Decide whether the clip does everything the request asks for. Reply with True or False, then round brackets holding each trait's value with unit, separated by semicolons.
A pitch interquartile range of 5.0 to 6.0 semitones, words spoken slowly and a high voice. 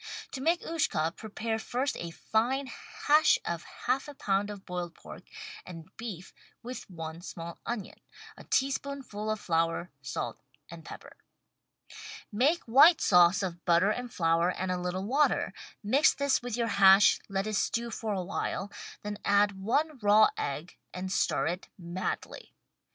False (5.4 semitones; 155 wpm; 205 Hz)